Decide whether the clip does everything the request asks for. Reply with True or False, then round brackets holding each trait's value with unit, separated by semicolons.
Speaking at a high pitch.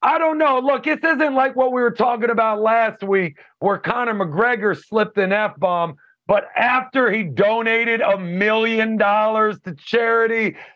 True (220 Hz)